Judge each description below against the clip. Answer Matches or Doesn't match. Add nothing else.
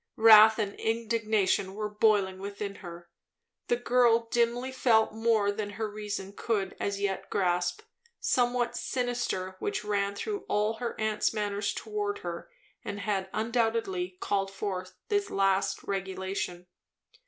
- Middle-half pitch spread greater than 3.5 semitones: Doesn't match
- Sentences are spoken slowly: Matches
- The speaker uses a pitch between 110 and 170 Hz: Doesn't match